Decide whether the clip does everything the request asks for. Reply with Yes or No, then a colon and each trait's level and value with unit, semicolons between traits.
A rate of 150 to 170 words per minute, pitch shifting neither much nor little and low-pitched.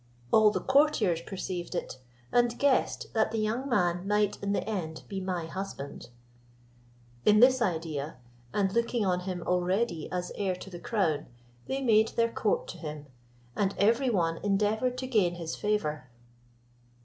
No: average, 160 wpm; average, 4.7 semitones; high, 200 Hz